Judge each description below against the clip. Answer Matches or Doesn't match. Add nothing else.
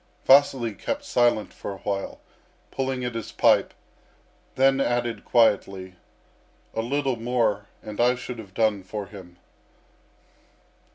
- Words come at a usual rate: Doesn't match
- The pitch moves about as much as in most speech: Matches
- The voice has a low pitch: Matches